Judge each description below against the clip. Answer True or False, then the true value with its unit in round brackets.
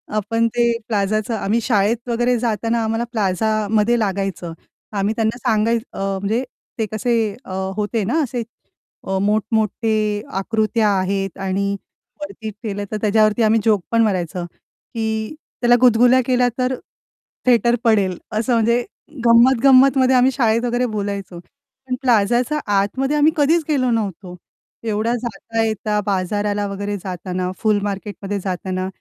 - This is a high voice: True (220 Hz)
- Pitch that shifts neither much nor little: True (3.1 semitones)